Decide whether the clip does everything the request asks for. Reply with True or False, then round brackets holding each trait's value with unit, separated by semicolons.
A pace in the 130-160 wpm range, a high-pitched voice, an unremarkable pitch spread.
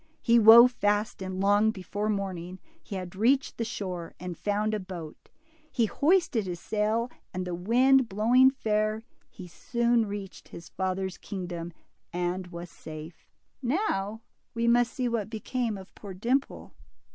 True (150 wpm; 210 Hz; 4.2 semitones)